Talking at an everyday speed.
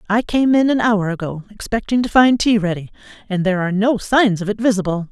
No: fast, 225 wpm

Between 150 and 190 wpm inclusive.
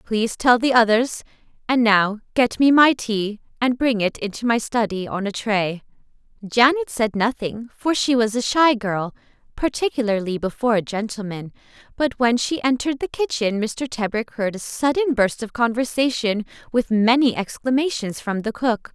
Yes: average, 160 wpm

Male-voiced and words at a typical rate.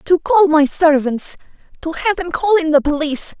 No: female; average, 175 wpm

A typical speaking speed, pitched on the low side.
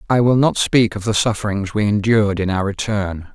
No: fast, 215 wpm; low, 105 Hz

